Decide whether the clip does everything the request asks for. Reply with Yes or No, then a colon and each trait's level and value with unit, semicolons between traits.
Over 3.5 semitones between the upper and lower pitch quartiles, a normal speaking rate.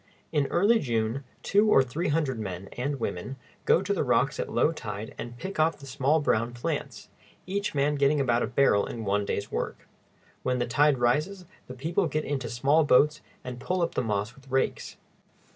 Yes: average, 4.3 semitones; average, 195 wpm